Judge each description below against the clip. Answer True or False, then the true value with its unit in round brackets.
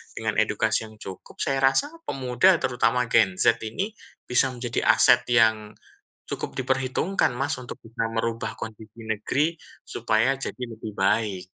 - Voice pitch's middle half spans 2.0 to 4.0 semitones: True (2.8 semitones)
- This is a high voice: False (115 Hz)